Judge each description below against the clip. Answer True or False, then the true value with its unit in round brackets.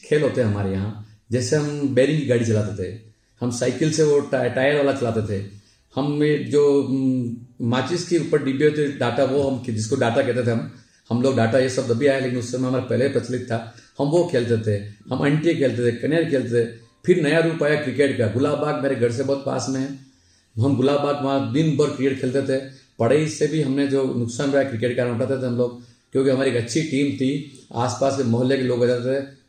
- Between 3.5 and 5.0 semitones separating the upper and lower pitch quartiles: False (2.9 semitones)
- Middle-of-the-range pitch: False (130 Hz)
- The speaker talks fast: True (235 wpm)